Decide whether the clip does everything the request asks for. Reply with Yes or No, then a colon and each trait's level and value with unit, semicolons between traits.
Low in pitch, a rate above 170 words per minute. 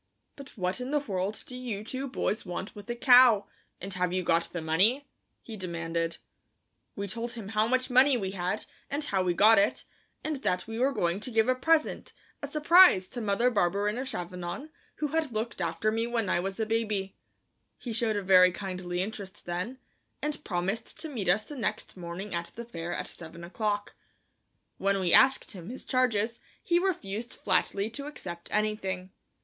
No: high, 210 Hz; average, 190 wpm